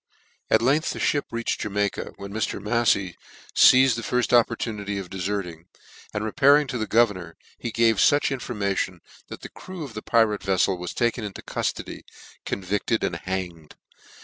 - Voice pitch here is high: No, low, 105 Hz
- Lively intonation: No, average, 3.6 semitones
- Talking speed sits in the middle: Yes, average, 160 wpm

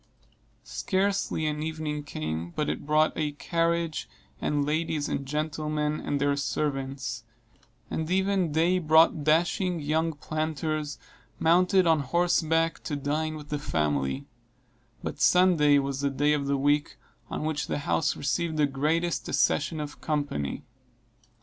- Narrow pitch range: Yes, narrow, 2.2 semitones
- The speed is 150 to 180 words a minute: No, slow, 135 wpm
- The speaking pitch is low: No, medium, 150 Hz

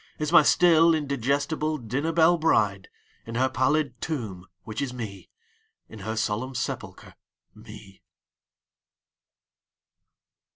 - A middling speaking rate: No, slow, 110 wpm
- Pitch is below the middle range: Yes, low, 130 Hz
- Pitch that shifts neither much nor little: No, wide, 5.9 semitones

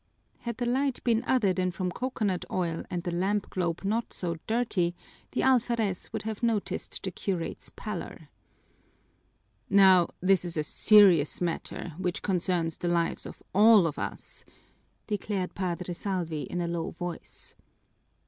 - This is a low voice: No, medium, 185 Hz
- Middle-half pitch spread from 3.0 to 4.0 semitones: Yes, average, 3.6 semitones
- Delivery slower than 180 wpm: Yes, average, 150 wpm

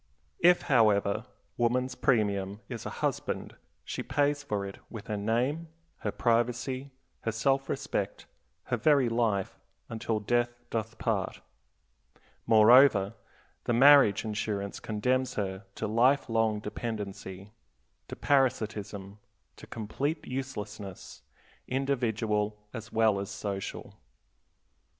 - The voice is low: Yes, low, 115 Hz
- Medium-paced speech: No, slow, 110 wpm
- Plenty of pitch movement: No, average, 3.7 semitones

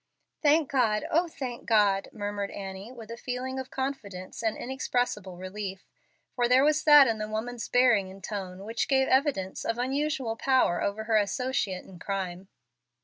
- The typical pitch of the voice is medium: No, high, 225 Hz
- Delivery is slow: No, average, 165 wpm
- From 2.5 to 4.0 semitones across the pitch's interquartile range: No, average, 4.8 semitones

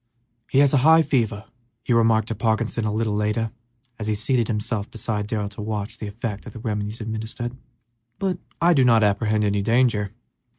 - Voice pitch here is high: No, low, 110 Hz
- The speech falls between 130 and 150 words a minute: No, average, 185 wpm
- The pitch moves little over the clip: Yes, narrow, 2.1 semitones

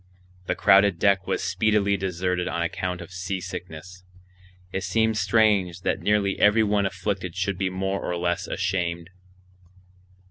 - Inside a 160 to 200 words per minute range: No, average, 140 wpm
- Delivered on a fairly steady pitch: Yes, narrow, 1.9 semitones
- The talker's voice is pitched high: No, very low, 95 Hz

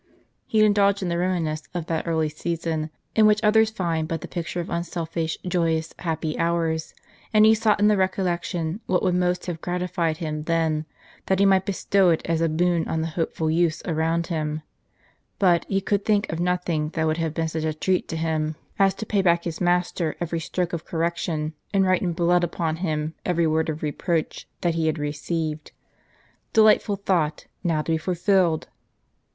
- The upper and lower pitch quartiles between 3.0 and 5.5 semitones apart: No, narrow, 2.5 semitones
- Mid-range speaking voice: Yes, medium, 170 Hz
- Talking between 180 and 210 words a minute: Yes, average, 190 wpm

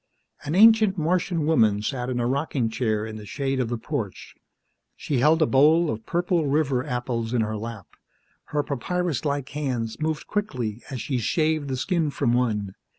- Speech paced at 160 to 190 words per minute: Yes, average, 180 wpm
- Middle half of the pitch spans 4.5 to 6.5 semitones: Yes, average, 5.2 semitones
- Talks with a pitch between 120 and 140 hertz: Yes, low, 135 Hz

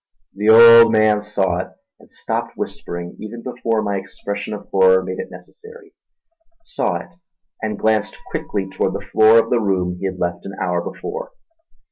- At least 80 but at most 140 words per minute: No, average, 170 wpm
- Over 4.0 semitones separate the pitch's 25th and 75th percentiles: No, average, 3.4 semitones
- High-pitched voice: No, low, 105 Hz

